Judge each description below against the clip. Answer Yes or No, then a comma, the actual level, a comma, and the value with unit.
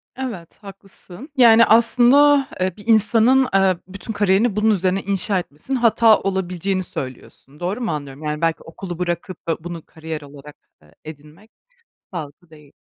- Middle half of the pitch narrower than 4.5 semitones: No, wide, 5.6 semitones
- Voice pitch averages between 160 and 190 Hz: Yes, medium, 185 Hz